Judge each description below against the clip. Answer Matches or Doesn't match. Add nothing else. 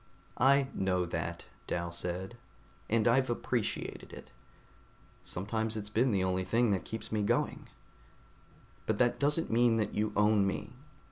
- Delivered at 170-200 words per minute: Doesn't match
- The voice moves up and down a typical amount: Matches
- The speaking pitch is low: Matches